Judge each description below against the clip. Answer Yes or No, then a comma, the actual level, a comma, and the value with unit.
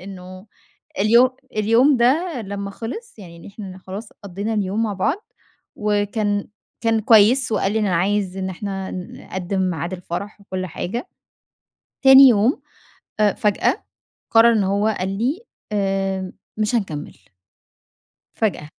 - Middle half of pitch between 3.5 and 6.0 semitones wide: No, average, 3.1 semitones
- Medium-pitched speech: No, high, 205 Hz